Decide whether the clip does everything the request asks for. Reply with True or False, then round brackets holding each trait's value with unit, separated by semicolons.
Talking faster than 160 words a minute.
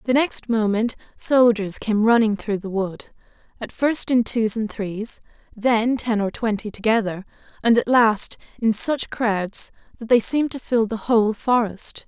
True (170 wpm)